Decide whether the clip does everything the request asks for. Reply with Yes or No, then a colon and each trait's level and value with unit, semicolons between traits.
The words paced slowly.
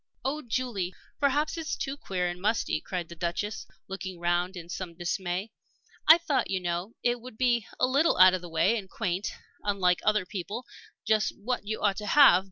No: average, 195 wpm